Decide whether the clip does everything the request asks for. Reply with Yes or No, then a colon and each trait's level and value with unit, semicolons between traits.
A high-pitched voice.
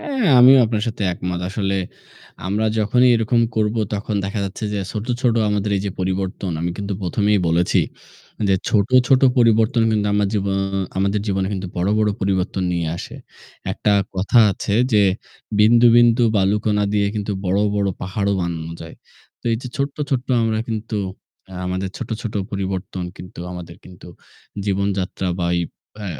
No: low, 100 Hz